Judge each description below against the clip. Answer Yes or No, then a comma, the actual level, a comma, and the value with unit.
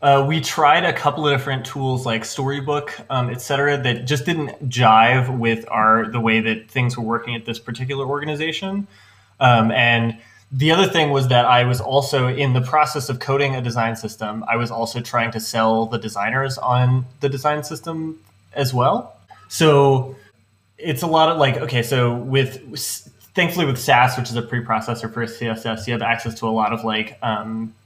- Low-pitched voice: Yes, low, 125 Hz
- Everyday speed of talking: Yes, average, 190 wpm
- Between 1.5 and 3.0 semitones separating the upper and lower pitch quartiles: No, average, 3.6 semitones